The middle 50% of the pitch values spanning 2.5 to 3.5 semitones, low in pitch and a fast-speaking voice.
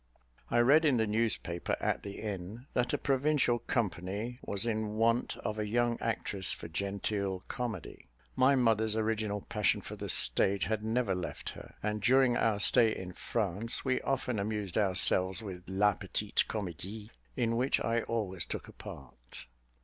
No: average, 3.2 semitones; low, 110 Hz; average, 165 wpm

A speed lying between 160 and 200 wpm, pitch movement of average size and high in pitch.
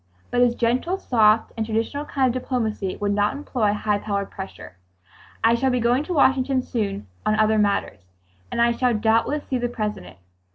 Yes: average, 180 wpm; average, 3.2 semitones; high, 230 Hz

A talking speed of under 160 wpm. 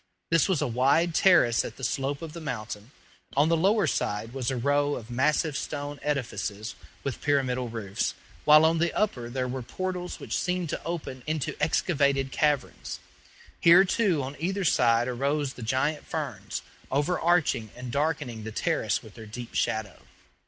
No: average, 165 wpm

